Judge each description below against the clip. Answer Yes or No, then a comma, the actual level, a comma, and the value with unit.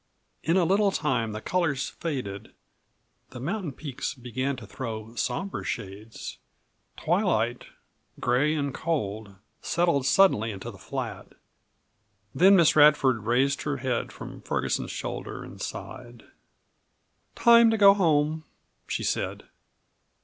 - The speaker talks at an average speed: No, slow, 120 wpm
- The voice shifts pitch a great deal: Yes, wide, 6.3 semitones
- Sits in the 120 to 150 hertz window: Yes, medium, 140 Hz